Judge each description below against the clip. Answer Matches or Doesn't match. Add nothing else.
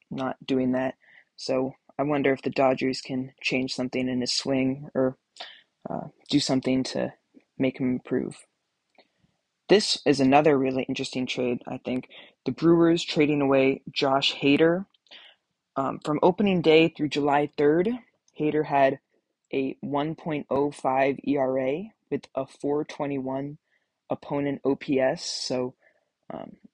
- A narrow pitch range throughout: Matches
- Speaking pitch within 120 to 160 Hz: Matches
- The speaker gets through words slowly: Matches